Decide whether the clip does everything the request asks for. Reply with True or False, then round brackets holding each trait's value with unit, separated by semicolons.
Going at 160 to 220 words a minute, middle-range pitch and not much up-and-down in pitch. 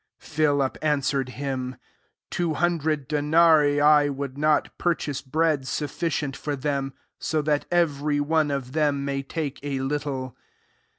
False (140 wpm; 145 Hz; 1.9 semitones)